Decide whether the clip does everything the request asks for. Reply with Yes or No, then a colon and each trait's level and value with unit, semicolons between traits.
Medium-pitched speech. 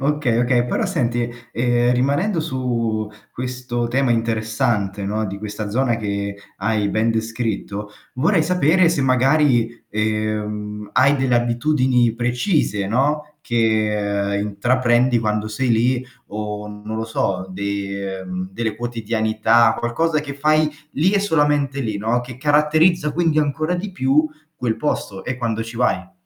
No: low, 120 Hz